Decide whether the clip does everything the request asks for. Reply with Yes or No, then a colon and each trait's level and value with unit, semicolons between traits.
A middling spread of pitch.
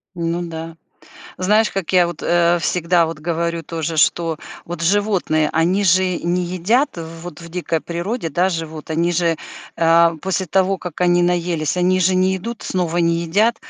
No: narrow, 2.0 semitones